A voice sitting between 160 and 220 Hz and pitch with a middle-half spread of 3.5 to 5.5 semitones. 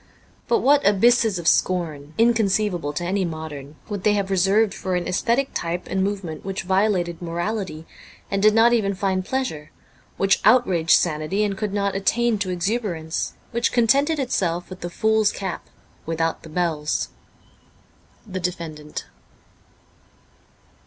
Yes: high, 190 Hz; average, 4.0 semitones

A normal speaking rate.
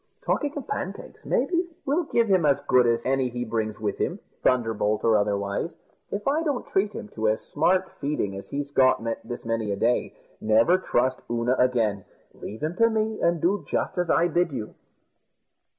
Yes: average, 185 wpm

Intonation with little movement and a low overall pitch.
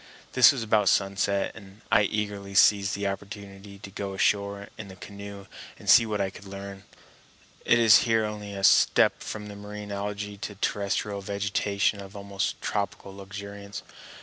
Yes: narrow, 0.9 semitones; low, 100 Hz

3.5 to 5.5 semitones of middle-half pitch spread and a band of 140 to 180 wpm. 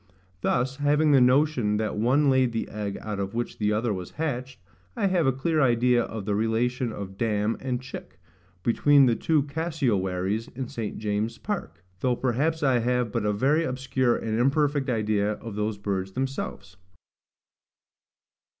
Yes: average, 4.2 semitones; average, 165 wpm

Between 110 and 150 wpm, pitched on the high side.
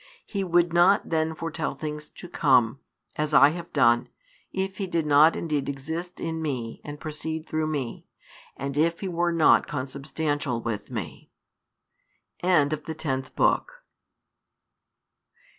No: average, 140 wpm; medium, 155 Hz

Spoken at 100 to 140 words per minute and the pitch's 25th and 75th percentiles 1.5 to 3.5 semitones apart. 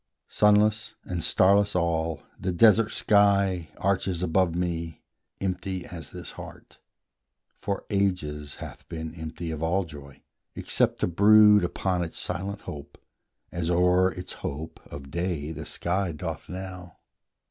Yes: slow, 135 wpm; average, 3.2 semitones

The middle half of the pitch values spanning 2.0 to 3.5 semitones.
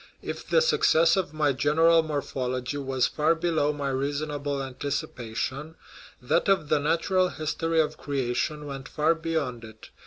Yes: average, 3.2 semitones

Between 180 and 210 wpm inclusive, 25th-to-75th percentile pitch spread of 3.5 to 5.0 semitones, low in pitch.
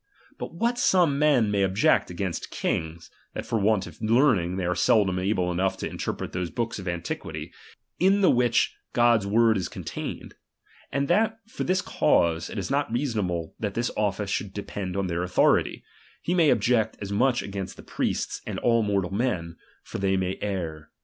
Yes: average, 185 wpm; average, 4.7 semitones; low, 100 Hz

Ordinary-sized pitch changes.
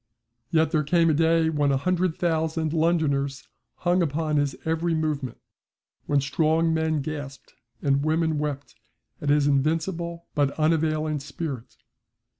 No: narrow, 2.2 semitones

